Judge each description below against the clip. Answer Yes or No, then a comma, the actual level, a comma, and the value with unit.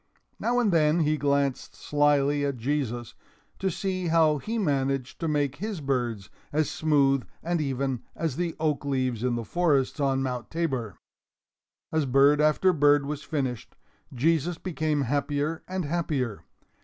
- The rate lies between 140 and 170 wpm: Yes, average, 150 wpm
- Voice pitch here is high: No, medium, 145 Hz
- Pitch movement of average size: Yes, average, 3.1 semitones